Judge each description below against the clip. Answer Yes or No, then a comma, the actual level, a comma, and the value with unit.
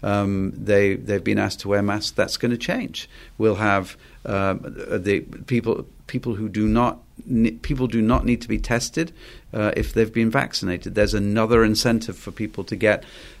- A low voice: Yes, low, 110 Hz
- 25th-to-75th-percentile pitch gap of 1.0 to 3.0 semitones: Yes, average, 2.7 semitones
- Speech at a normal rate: Yes, average, 195 wpm